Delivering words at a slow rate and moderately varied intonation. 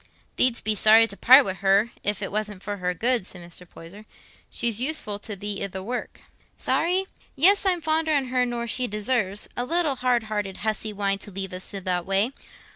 No: average, 200 wpm; average, 4.3 semitones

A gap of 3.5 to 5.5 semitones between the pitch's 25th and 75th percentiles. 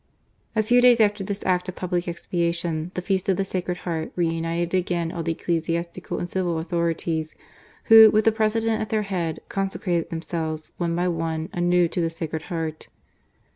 No: average, 2.7 semitones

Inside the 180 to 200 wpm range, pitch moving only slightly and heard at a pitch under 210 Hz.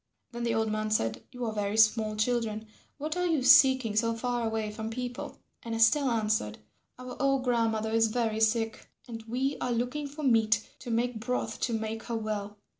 No: average, 190 wpm; narrow, 2.2 semitones; high, 225 Hz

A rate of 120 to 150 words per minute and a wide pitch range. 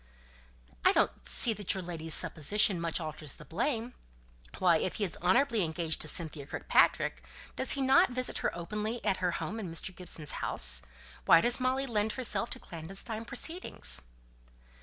No: average, 165 wpm; wide, 5.8 semitones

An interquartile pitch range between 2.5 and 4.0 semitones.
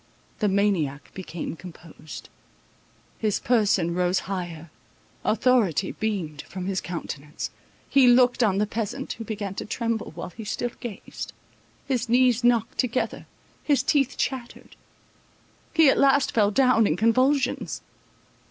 No: average, 5.3 semitones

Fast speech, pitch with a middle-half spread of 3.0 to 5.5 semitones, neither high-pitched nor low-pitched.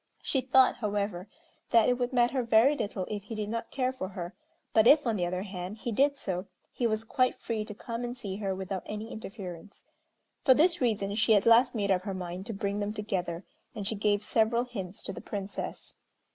No: fast, 215 wpm; average, 3.6 semitones; high, 215 Hz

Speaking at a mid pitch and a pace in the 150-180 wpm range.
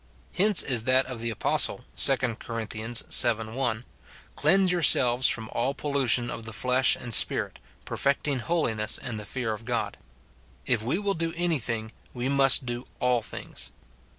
No: low, 125 Hz; average, 170 wpm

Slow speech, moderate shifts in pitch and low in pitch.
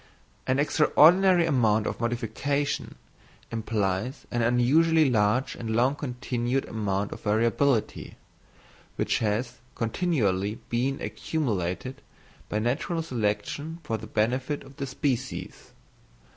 Yes: slow, 105 wpm; average, 4.4 semitones; low, 125 Hz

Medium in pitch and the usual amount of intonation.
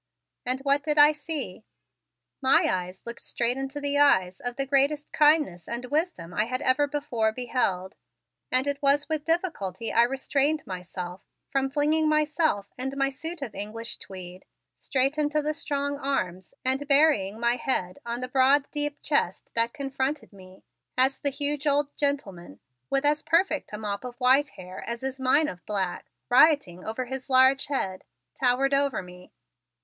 No: very high, 265 Hz; average, 4.9 semitones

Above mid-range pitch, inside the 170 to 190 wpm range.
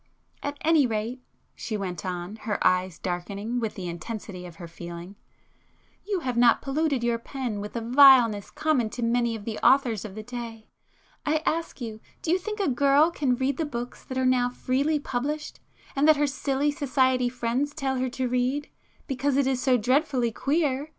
Yes: very high, 250 Hz; average, 180 wpm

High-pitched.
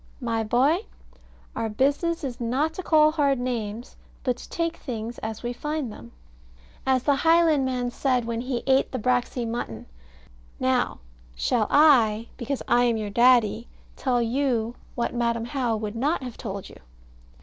Yes: high, 245 Hz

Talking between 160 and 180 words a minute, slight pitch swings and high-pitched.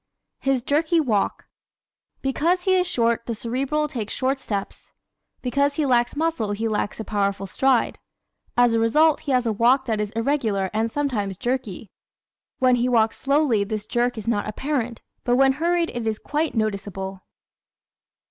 No: average, 165 wpm; average, 4.5 semitones; high, 245 Hz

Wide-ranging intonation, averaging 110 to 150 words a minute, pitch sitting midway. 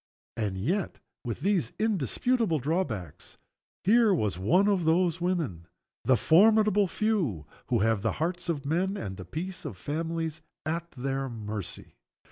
Yes: wide, 8.8 semitones; average, 140 wpm; medium, 160 Hz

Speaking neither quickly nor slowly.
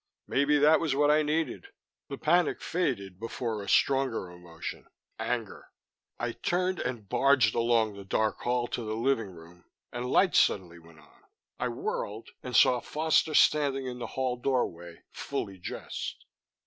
Yes: average, 155 wpm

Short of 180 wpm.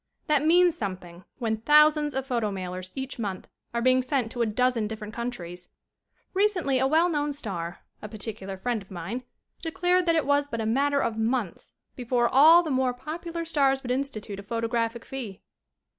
No: average, 185 wpm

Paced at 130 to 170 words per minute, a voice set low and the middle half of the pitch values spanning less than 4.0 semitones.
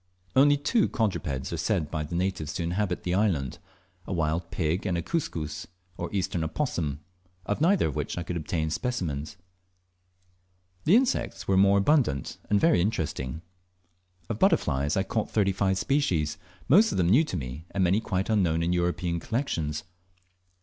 No: average, 165 wpm; very low, 90 Hz; average, 4.8 semitones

